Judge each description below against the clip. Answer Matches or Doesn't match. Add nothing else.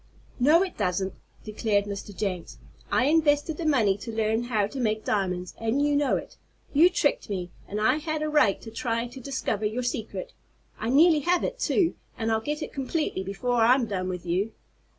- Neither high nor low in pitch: Doesn't match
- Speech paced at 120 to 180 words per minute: Doesn't match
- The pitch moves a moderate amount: Doesn't match